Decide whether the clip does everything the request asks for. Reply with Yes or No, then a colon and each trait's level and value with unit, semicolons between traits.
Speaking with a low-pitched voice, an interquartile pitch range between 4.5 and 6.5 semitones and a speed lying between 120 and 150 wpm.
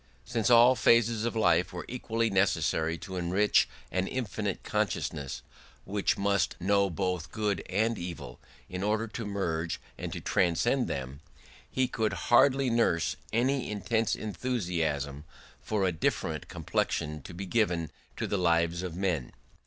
Yes: low, 100 Hz; average, 5.0 semitones; average, 145 wpm